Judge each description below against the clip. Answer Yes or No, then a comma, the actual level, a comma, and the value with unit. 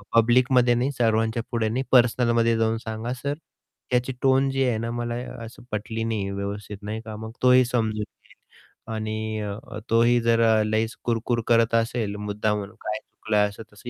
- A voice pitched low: Yes, low, 115 Hz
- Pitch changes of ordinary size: No, narrow, 1.8 semitones